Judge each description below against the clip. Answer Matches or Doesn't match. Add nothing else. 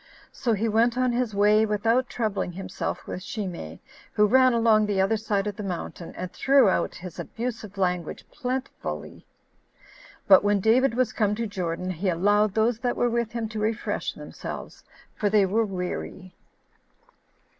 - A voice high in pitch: Matches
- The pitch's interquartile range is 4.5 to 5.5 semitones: Doesn't match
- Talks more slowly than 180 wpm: Matches